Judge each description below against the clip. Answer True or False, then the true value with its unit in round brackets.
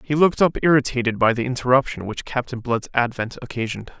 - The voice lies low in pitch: True (125 Hz)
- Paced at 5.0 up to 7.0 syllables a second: True (6.5 syllables/s)